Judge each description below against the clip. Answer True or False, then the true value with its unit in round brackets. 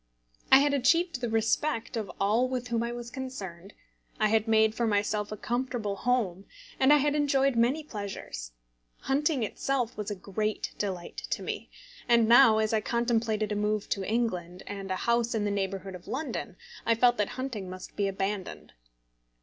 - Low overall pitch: False (220 Hz)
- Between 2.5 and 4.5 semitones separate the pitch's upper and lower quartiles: True (3.6 semitones)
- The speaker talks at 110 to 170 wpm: False (180 wpm)